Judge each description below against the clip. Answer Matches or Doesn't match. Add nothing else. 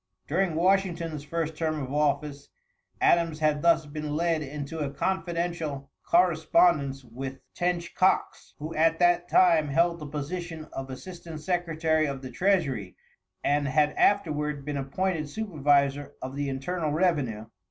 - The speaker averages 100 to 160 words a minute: Matches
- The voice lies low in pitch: Doesn't match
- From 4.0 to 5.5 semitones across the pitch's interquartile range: Doesn't match